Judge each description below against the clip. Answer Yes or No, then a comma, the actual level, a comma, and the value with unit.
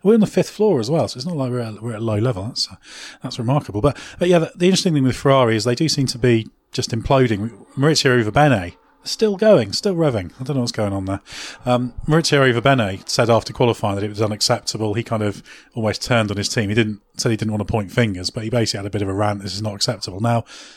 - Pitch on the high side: No, low, 120 Hz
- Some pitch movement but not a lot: Yes, average, 4.4 semitones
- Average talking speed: No, fast, 270 wpm